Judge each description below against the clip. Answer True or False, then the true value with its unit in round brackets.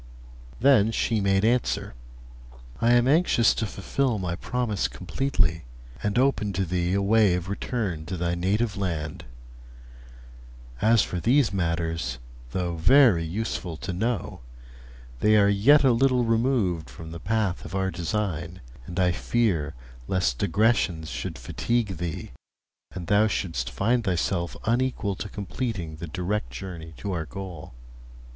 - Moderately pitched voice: False (95 Hz)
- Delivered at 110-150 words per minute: True (140 wpm)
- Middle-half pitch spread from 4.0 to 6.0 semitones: True (4.8 semitones)